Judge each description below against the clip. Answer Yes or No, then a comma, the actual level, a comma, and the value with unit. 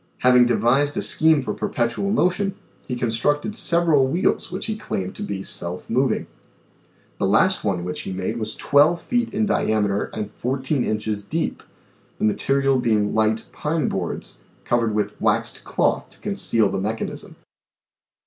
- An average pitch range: No, wide, 6.0 semitones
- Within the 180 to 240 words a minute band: No, average, 160 wpm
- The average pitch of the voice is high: No, low, 120 Hz